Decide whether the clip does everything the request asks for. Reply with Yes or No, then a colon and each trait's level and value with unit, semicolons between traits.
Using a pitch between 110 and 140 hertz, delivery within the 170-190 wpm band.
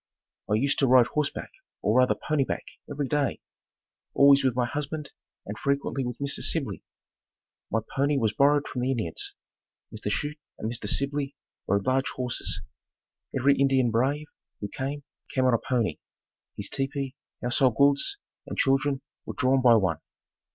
No: low, 135 Hz; average, 160 wpm